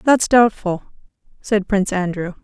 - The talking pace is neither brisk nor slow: Yes, average, 150 wpm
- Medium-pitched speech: No, high, 200 Hz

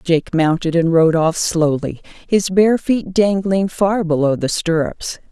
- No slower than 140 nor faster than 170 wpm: Yes, average, 160 wpm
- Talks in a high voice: No, medium, 175 Hz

